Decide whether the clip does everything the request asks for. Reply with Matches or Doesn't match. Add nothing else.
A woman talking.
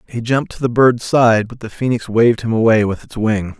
Doesn't match